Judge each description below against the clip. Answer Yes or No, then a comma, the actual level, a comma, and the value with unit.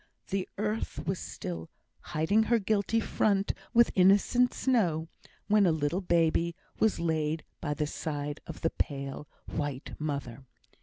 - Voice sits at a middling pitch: Yes, medium, 165 Hz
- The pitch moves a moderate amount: No, wide, 5.7 semitones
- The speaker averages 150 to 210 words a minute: No, average, 140 wpm